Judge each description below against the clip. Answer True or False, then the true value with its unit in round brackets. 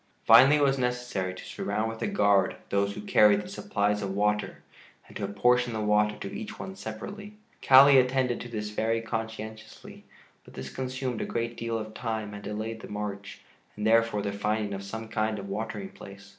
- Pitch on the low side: True (110 Hz)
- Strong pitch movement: False (3.0 semitones)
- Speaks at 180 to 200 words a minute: True (195 wpm)